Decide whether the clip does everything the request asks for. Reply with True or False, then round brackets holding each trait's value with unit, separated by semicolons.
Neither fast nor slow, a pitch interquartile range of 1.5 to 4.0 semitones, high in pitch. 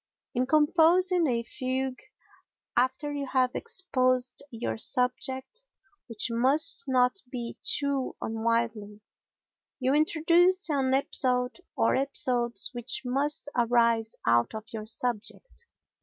False (110 wpm; 3.5 semitones; 255 Hz)